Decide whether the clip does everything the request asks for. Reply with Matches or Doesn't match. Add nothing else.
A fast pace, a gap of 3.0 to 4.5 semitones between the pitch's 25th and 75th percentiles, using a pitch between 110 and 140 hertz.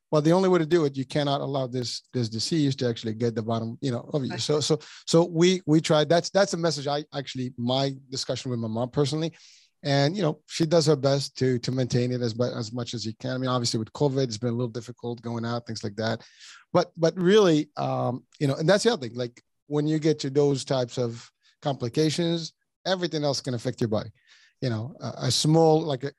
Matches